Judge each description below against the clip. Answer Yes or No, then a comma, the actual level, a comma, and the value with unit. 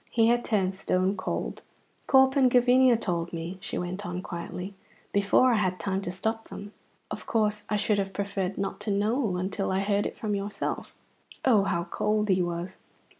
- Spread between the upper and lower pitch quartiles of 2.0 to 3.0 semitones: Yes, average, 2.7 semitones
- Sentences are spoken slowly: No, average, 185 wpm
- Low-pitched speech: No, high, 200 Hz